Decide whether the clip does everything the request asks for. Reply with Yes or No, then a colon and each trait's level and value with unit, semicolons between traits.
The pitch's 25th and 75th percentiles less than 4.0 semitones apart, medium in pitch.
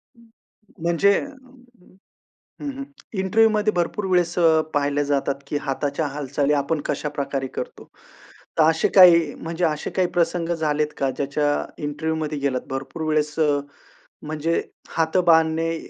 Yes: average, 2.9 semitones; medium, 155 Hz